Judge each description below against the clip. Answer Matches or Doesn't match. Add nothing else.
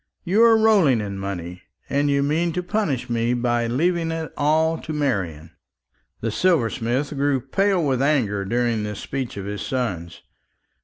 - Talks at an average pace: Matches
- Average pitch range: Doesn't match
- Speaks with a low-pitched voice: Matches